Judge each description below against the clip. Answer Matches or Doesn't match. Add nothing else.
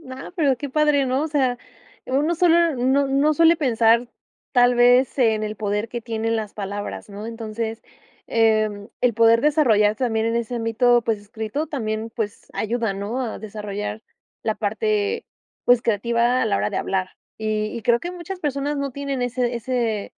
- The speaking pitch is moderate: Doesn't match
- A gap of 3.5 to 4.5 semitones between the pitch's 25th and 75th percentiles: Matches